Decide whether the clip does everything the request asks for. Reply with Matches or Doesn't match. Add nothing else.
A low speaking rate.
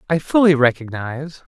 Matches